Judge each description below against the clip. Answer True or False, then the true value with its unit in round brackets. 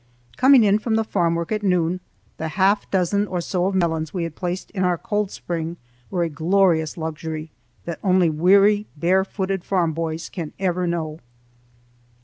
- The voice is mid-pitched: True (180 Hz)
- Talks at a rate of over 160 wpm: True (170 wpm)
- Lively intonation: False (3.0 semitones)